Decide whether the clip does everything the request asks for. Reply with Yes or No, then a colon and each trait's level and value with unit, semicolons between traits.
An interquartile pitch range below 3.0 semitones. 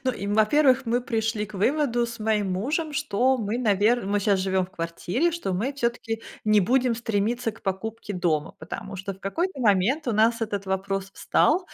No: average, 4.0 semitones